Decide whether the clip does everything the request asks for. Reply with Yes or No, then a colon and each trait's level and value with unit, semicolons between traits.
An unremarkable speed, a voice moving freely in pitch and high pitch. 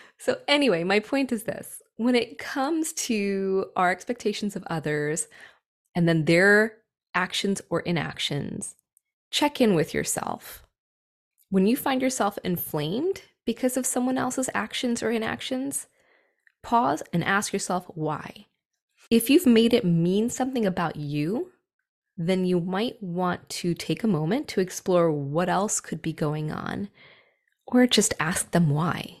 Yes: average, 145 wpm; wide, 6.2 semitones; high, 200 Hz